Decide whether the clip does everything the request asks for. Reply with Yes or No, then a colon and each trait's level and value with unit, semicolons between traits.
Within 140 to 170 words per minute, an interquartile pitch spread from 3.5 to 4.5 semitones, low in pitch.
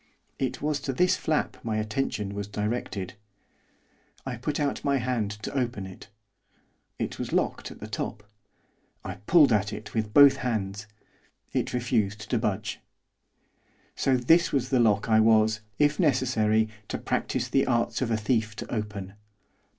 Yes: average, 160 wpm; average, 4.0 semitones; low, 115 Hz